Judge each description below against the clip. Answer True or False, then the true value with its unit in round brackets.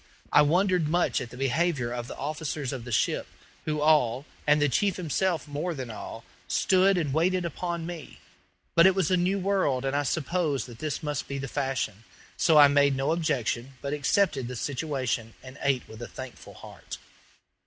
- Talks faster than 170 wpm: True (190 wpm)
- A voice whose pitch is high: False (145 Hz)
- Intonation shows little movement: False (4.5 semitones)